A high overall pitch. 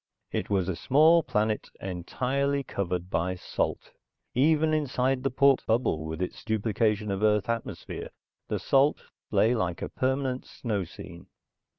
No: low, 110 Hz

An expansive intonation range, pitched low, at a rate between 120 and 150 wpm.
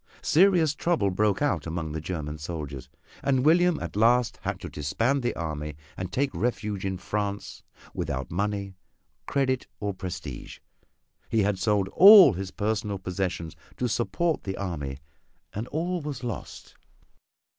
Yes: wide, 6.6 semitones; low, 105 Hz; average, 145 wpm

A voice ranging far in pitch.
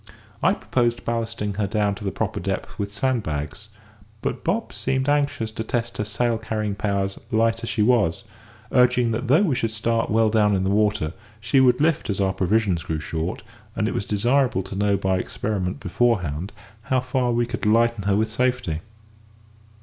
No: average, 3.3 semitones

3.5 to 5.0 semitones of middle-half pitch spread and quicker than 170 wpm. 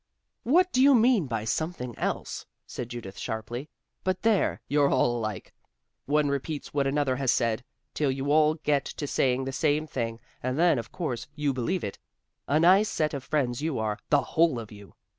Yes: average, 4.6 semitones; average, 190 wpm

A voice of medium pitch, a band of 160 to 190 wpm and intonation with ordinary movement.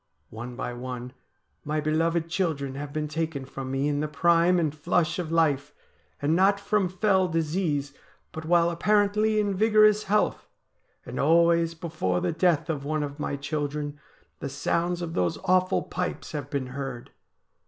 Yes: medium, 160 Hz; average, 165 wpm; average, 3.7 semitones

